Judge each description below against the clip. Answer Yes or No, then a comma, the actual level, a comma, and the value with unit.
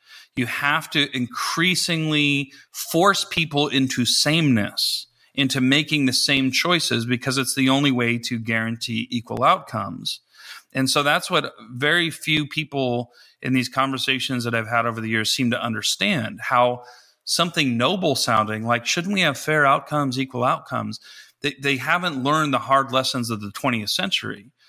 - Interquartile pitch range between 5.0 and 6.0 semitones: No, average, 3.4 semitones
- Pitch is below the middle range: Yes, low, 130 Hz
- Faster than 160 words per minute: No, average, 155 wpm